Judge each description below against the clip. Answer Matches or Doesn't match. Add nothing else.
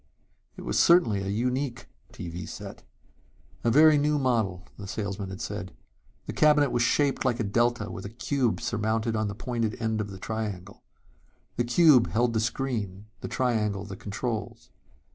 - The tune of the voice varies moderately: Matches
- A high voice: Doesn't match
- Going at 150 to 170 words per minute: Matches